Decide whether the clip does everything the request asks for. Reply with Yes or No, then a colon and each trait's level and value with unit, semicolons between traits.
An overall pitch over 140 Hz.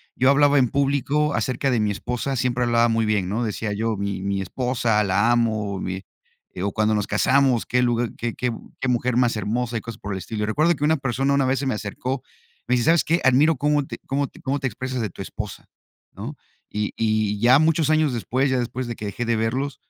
No: low, 120 Hz